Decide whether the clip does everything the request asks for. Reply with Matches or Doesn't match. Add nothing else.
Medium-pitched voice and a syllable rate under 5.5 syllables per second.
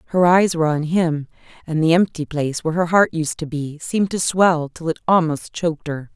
Doesn't match